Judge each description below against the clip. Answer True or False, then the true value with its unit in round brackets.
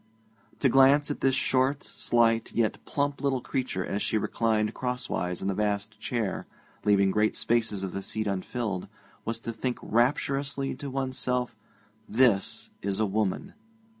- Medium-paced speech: True (155 wpm)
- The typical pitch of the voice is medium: False (115 Hz)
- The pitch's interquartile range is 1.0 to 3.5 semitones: False (4.2 semitones)